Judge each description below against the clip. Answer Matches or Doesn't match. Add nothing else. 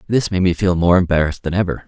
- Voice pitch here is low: Matches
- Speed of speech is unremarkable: Doesn't match